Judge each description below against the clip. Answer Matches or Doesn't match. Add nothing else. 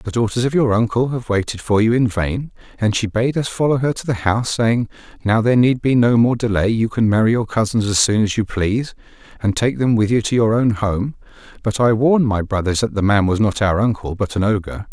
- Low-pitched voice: Matches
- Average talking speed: Doesn't match